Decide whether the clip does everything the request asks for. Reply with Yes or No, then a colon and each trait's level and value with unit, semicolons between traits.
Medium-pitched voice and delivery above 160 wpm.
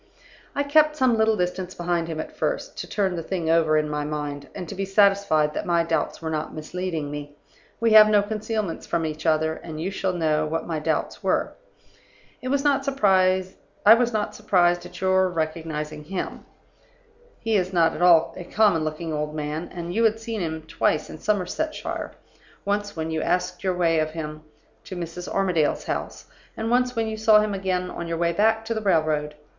Yes: medium, 180 Hz; average, 195 wpm